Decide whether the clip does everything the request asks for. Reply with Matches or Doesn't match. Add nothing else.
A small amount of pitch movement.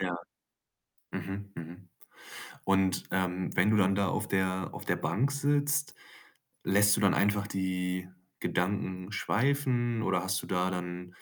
Matches